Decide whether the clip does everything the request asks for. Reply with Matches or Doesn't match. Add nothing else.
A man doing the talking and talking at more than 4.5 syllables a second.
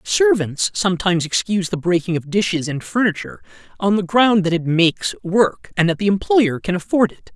Matches